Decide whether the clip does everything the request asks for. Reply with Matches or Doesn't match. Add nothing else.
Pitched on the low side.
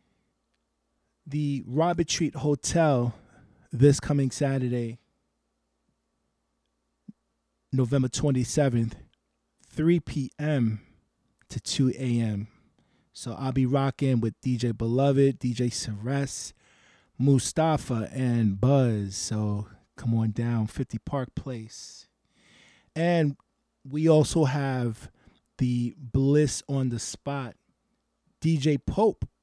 Matches